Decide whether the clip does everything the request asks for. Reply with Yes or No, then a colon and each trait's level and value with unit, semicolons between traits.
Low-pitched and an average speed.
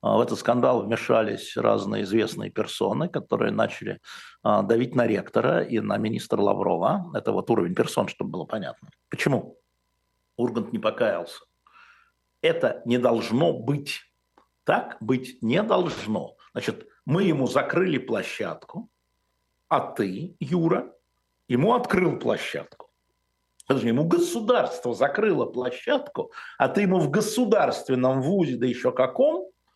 Yes: low, 130 Hz; average, 120 wpm